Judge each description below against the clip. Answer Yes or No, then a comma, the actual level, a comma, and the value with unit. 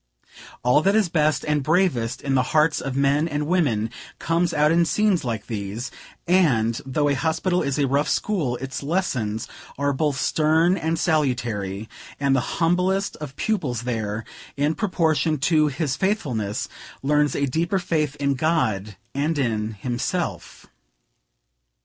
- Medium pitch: Yes, medium, 145 Hz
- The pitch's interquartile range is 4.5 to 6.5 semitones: Yes, average, 4.9 semitones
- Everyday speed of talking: Yes, average, 150 wpm